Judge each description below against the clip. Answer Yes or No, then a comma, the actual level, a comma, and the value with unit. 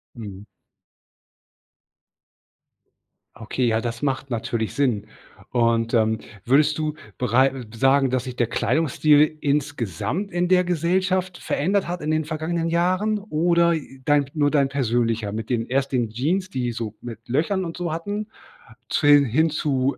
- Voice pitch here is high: No, medium, 140 Hz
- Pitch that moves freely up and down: Yes, wide, 5.7 semitones